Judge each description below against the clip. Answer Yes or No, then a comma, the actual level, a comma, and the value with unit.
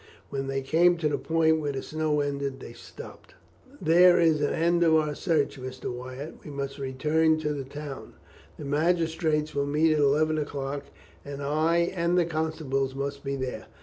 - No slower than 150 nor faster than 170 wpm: No, average, 180 wpm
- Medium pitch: Yes, medium, 150 Hz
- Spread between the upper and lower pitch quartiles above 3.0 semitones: No, narrow, 2.5 semitones